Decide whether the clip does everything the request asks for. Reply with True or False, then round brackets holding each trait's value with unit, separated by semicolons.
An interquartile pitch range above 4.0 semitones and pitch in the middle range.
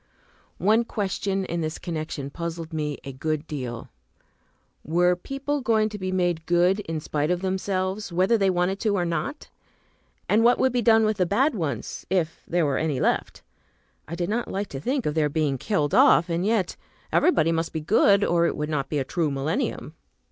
True (4.7 semitones; 175 Hz)